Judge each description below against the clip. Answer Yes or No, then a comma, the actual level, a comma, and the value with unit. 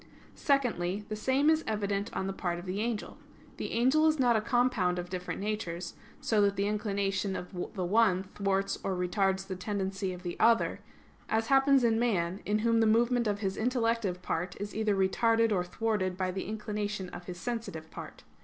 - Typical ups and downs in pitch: Yes, average, 3.4 semitones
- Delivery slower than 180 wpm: No, average, 190 wpm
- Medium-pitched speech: No, high, 205 Hz